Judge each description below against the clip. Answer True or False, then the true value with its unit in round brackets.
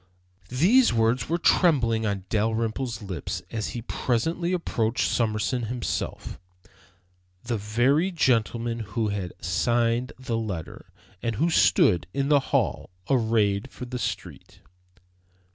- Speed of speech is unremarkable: False (120 wpm)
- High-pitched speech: False (115 Hz)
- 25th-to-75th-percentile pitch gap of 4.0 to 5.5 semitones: False (3.2 semitones)